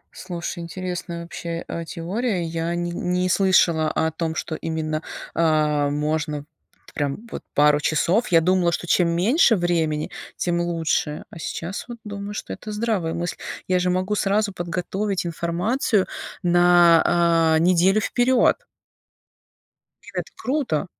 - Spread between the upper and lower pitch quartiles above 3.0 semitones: No, narrow, 2.6 semitones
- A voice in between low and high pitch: Yes, medium, 175 Hz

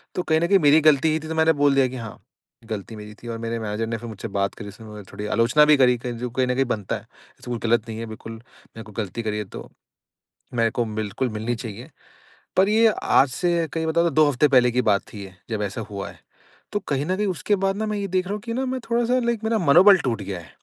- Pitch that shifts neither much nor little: No, wide, 7.2 semitones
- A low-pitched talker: Yes, low, 125 Hz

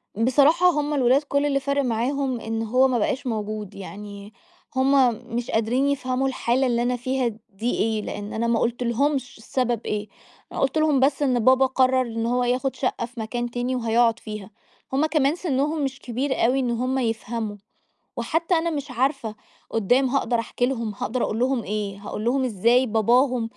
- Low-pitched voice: No, high, 245 Hz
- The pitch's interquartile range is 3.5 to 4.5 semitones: No, average, 3.0 semitones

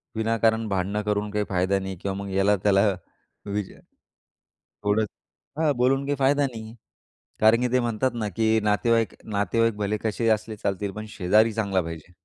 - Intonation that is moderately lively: No, narrow, 2.3 semitones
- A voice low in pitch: Yes, low, 105 Hz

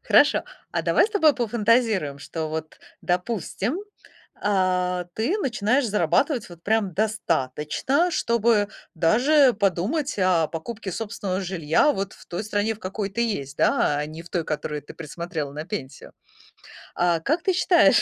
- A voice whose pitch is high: Yes, high, 195 Hz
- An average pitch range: No, wide, 6.0 semitones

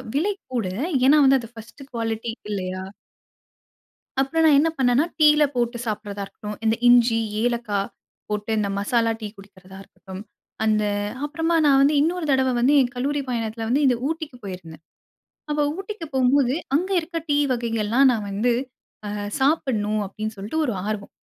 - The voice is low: No, high, 240 Hz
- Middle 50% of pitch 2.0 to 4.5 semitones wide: No, average, 5.2 semitones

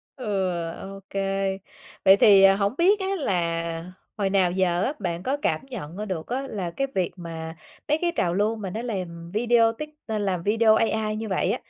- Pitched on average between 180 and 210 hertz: Yes, high, 195 Hz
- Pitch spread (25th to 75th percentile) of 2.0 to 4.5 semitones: Yes, average, 4.1 semitones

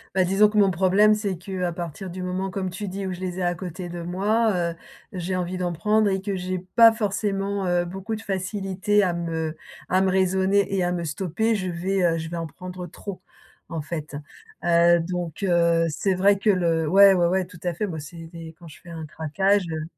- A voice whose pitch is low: No, medium, 185 Hz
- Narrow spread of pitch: Yes, narrow, 2.3 semitones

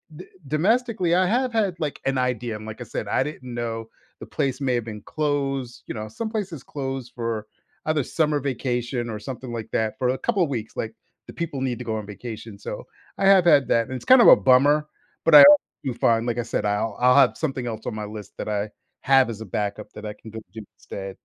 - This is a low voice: Yes, low, 125 Hz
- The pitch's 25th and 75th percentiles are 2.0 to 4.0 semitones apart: No, average, 5.1 semitones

